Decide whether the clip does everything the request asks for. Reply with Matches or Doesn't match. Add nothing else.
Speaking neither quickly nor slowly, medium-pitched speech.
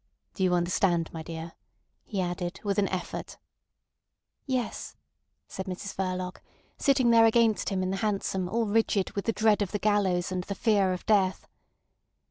Doesn't match